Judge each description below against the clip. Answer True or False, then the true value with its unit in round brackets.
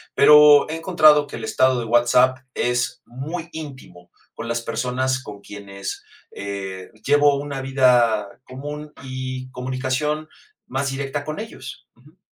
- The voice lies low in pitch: True (130 Hz)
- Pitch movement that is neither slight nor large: True (3.4 semitones)